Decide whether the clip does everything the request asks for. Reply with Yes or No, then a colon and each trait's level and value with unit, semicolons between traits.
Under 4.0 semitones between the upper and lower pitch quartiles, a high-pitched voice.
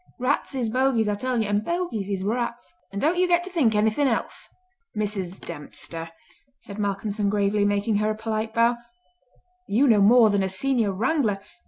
Yes: average, 3.6 semitones; high, 215 Hz